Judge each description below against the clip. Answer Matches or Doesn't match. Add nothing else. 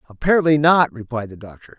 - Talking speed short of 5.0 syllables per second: Doesn't match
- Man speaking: Matches